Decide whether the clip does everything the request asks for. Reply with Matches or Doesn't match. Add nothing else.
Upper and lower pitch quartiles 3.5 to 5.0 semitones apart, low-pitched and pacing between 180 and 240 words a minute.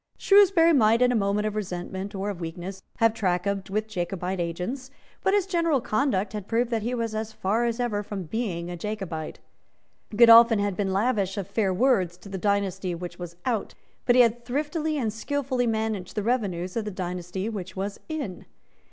Doesn't match